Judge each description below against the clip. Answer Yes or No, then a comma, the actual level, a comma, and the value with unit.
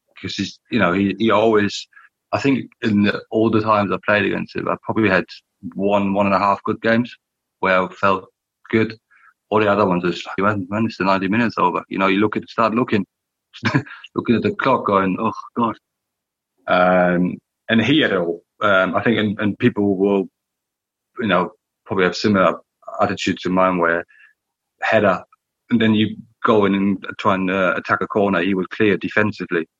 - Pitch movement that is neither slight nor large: No, narrow, 2.3 semitones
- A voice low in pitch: Yes, low, 100 Hz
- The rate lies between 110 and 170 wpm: No, average, 195 wpm